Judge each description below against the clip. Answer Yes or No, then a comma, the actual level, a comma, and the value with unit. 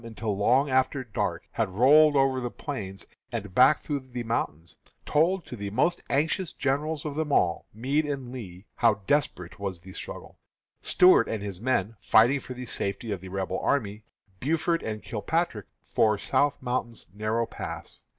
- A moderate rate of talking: Yes, average, 170 wpm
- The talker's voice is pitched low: Yes, low, 120 Hz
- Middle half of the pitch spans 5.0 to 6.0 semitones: Yes, wide, 5.6 semitones